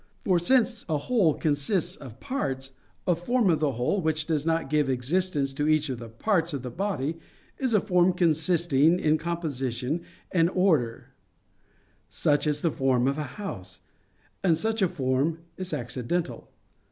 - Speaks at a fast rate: No, average, 165 wpm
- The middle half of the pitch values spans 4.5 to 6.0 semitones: Yes, average, 4.9 semitones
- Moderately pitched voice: Yes, medium, 155 Hz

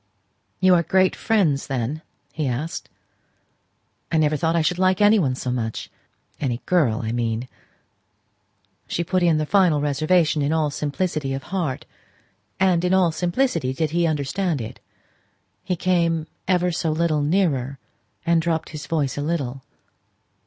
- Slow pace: No, average, 150 wpm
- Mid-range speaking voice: Yes, medium, 160 Hz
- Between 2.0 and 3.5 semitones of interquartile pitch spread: No, average, 4.1 semitones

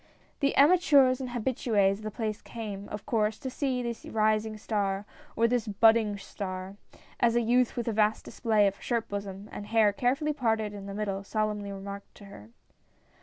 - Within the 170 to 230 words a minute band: Yes, average, 180 wpm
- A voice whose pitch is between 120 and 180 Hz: No, high, 215 Hz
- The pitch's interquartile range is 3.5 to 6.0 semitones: No, average, 2.9 semitones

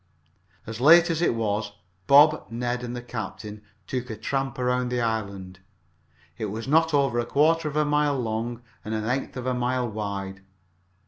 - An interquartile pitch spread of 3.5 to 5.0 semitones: Yes, average, 4.0 semitones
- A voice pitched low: Yes, low, 120 Hz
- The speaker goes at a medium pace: Yes, average, 180 wpm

